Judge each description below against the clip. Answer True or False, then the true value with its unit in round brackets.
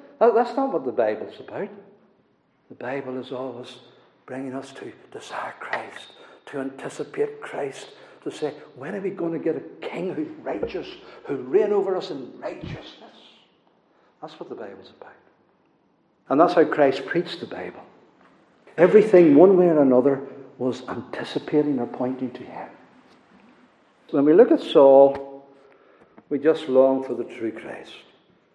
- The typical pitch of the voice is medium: True (145 Hz)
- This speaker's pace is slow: False (150 wpm)